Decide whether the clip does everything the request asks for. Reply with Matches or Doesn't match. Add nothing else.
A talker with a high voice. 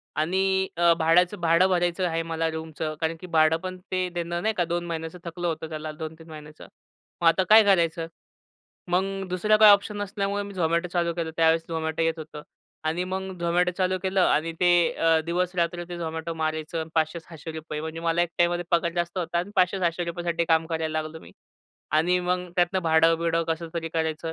Doesn't match